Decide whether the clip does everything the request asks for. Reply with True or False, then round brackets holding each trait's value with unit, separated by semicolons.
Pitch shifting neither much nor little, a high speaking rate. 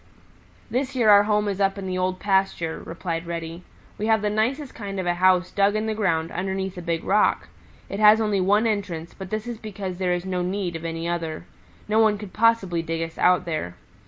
True (3.4 semitones; 220 wpm)